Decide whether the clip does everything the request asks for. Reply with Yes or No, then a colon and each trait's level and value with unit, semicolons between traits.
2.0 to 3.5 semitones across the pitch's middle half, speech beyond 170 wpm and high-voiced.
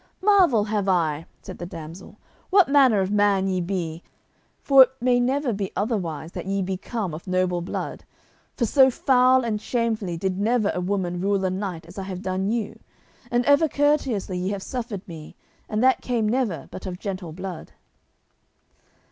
No: average, 4.9 semitones; average, 180 wpm; high, 200 Hz